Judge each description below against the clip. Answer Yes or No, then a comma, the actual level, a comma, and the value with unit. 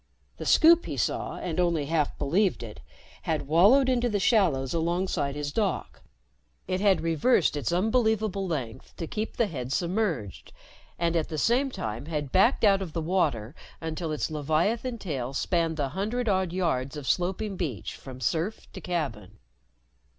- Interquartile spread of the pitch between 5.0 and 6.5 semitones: Yes, wide, 5.4 semitones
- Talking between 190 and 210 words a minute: No, average, 165 wpm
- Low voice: No, medium, 170 Hz